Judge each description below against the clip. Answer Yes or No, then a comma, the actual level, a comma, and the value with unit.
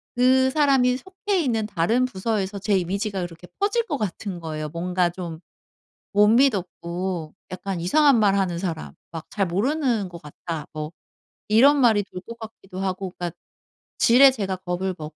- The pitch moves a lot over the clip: Yes, wide, 5.7 semitones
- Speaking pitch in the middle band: No, high, 195 Hz